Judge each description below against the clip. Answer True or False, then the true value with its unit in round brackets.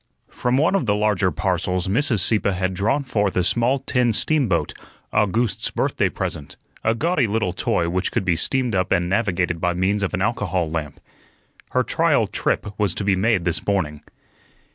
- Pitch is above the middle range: False (100 Hz)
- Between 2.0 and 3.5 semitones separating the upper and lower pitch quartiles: False (4.3 semitones)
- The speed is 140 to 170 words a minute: False (180 wpm)